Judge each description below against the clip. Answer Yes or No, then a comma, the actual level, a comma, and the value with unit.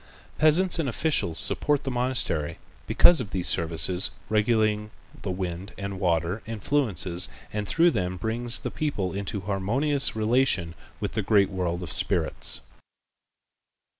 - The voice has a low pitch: Yes, low, 105 Hz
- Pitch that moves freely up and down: Yes, wide, 5.8 semitones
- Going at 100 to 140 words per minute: Yes, slow, 135 wpm